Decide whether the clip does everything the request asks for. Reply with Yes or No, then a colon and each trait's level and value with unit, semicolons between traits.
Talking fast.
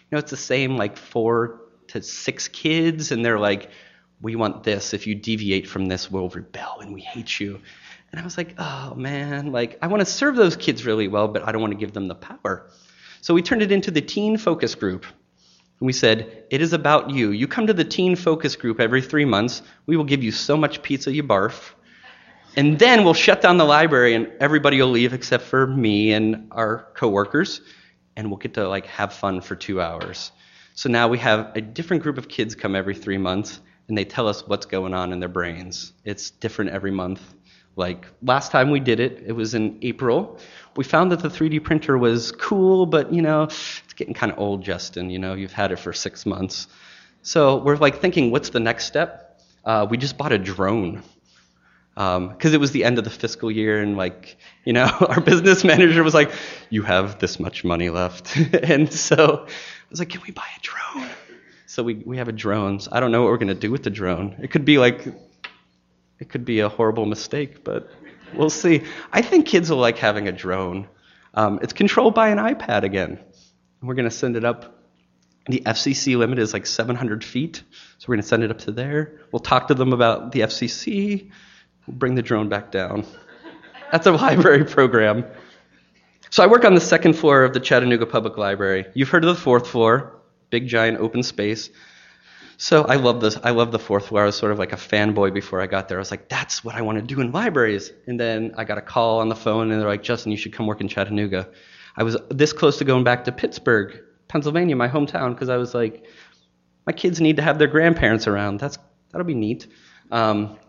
Yes: fast, 220 wpm